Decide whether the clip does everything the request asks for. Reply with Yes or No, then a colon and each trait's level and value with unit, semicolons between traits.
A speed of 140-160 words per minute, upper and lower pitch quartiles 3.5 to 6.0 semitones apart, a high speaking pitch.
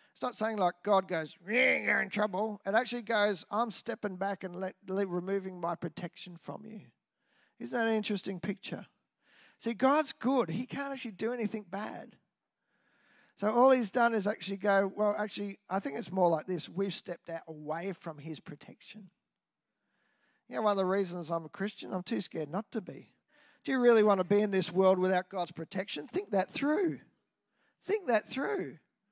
No: average, 190 wpm; average, 4.0 semitones; high, 205 Hz